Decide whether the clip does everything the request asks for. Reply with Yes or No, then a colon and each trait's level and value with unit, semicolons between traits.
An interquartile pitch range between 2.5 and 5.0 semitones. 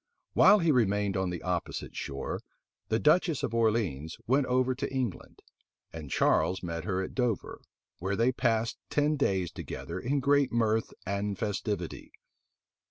No: wide, 5.5 semitones